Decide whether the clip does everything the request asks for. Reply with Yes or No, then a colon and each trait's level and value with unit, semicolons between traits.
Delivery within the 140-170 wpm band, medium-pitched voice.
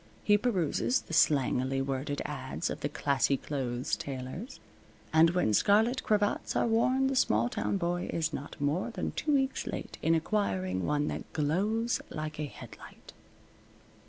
Yes: average, 155 wpm; medium, 160 Hz